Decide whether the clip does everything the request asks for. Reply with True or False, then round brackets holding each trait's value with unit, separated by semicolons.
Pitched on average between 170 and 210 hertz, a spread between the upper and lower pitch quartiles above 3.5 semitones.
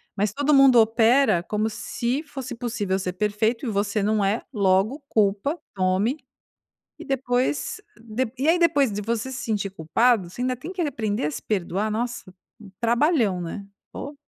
False (225 Hz; 4.6 semitones)